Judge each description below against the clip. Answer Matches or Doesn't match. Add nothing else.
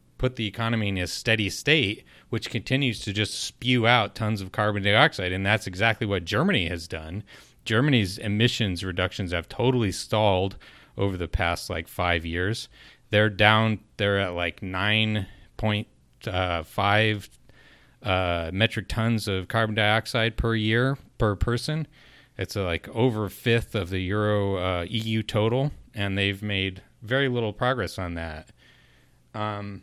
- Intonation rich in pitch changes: Doesn't match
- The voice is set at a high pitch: Doesn't match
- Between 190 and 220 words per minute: Doesn't match